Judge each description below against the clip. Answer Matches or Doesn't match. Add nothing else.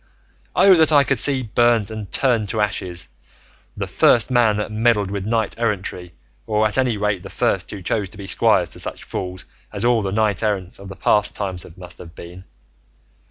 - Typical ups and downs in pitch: Matches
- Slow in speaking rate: Doesn't match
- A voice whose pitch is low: Matches